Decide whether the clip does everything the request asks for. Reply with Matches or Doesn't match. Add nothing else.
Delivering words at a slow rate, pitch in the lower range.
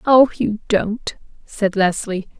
Doesn't match